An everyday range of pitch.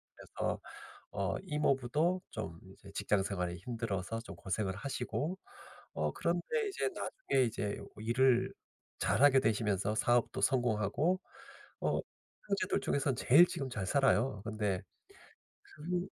No: wide, 6.4 semitones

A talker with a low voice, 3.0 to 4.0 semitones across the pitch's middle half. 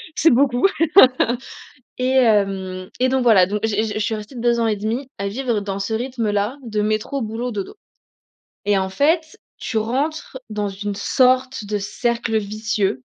No: high, 220 Hz; average, 3.7 semitones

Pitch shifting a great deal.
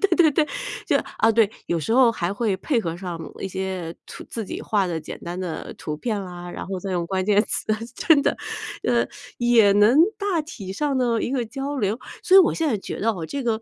Yes: wide, 5.8 semitones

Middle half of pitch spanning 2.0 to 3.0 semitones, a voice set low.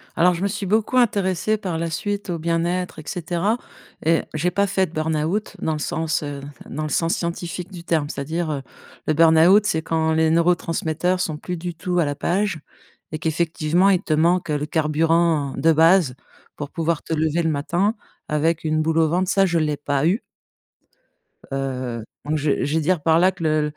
No: narrow, 2.5 semitones; medium, 165 Hz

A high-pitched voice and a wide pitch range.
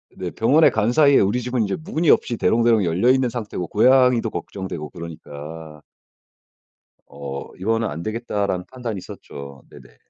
No: low, 105 Hz; wide, 6.7 semitones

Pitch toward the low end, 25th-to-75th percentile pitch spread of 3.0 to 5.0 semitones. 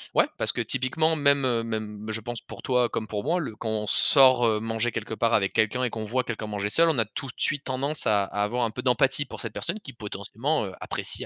Yes: low, 115 Hz; average, 3.6 semitones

